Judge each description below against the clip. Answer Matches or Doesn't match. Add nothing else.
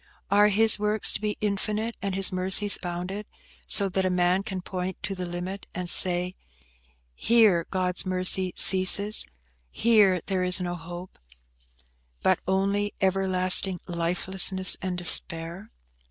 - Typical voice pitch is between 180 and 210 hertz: Matches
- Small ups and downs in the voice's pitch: Matches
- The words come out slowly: Matches